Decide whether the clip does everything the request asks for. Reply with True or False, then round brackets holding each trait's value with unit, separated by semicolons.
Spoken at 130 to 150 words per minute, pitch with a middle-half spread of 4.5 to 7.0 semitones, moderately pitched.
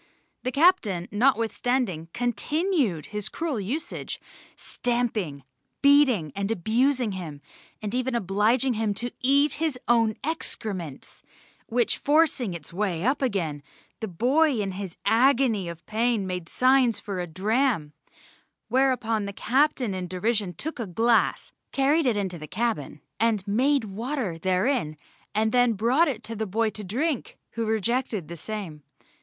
False (140 wpm; 5.2 semitones; 225 Hz)